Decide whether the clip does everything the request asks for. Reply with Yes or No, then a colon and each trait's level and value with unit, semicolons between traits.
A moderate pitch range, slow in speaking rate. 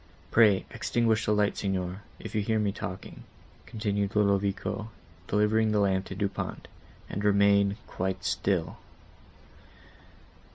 No: narrow, 1.4 semitones; slow, 125 wpm